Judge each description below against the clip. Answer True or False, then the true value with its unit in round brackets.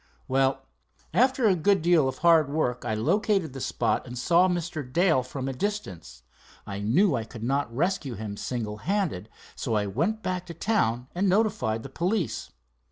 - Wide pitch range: True (7.6 semitones)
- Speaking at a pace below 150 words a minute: False (175 wpm)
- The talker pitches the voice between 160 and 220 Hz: False (150 Hz)